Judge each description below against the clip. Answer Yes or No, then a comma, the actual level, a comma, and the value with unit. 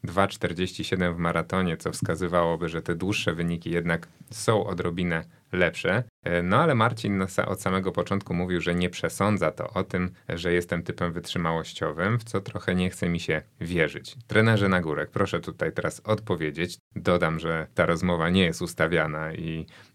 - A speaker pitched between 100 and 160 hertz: No, very low, 90 Hz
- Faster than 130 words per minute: Yes, fast, 160 wpm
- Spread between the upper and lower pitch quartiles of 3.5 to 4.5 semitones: No, narrow, 2.5 semitones